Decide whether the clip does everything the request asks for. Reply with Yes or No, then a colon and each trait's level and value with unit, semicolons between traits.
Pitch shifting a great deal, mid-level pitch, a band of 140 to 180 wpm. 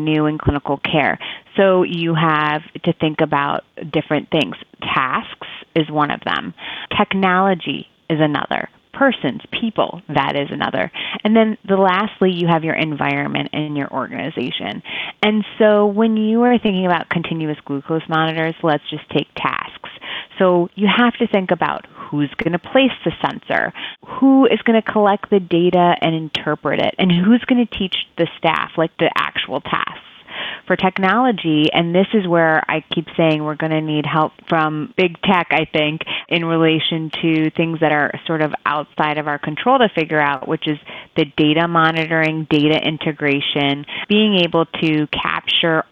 No: average, 3.9 semitones; medium, 165 Hz; average, 170 wpm